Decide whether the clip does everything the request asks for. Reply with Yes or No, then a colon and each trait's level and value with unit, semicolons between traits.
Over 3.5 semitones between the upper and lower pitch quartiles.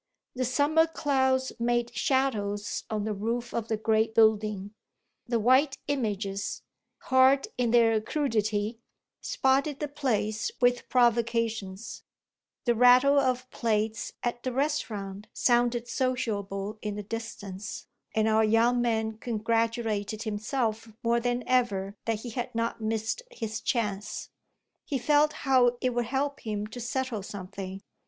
No: average, 2.9 semitones